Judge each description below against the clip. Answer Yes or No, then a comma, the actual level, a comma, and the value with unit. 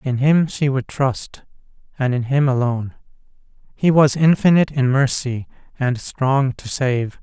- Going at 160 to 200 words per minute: No, average, 150 wpm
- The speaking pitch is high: No, low, 135 Hz